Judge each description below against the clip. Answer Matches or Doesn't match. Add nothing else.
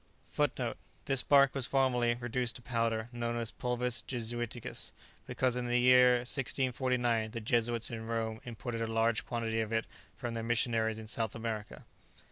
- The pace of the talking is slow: Doesn't match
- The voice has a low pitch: Matches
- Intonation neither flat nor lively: Doesn't match